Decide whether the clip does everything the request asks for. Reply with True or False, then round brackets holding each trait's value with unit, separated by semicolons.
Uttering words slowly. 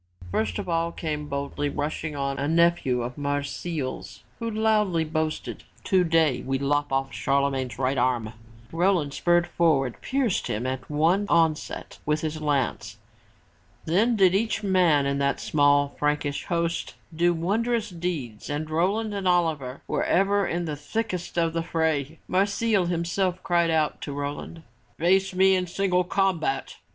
False (150 wpm)